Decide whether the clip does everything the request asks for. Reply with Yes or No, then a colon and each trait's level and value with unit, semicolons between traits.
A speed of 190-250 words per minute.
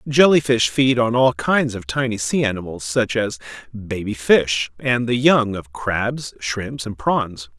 No: average, 175 wpm